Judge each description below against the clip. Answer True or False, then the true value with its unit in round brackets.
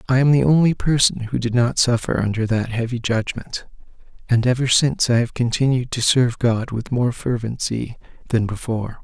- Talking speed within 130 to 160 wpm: False (180 wpm)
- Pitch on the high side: False (120 Hz)